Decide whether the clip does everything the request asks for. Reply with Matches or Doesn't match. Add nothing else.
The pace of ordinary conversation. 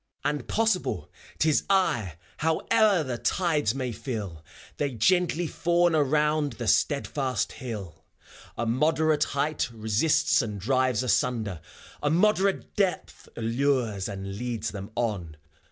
Doesn't match